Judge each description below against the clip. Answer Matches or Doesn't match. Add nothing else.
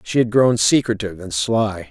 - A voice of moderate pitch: Doesn't match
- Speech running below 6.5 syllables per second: Matches